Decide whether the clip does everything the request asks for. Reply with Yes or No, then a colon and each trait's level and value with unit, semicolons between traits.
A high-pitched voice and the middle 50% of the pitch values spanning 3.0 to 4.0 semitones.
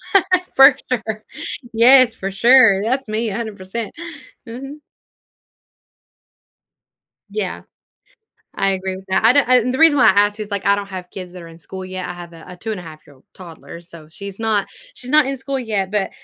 No: high, 205 Hz; average, 4.7 semitones